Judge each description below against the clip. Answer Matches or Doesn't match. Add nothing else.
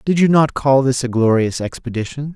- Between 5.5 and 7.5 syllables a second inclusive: Doesn't match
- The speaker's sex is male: Matches